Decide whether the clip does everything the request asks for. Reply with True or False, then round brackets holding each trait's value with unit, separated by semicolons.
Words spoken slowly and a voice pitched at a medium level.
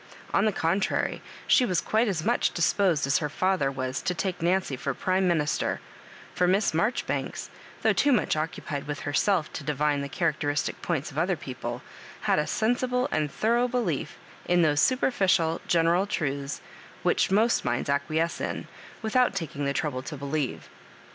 False (165 wpm; 165 Hz)